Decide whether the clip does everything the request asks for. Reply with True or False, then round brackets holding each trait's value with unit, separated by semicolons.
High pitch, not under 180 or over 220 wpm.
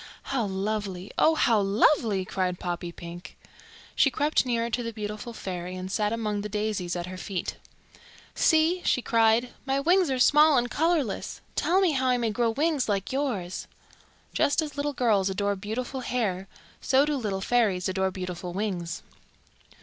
False (220 Hz; 165 wpm)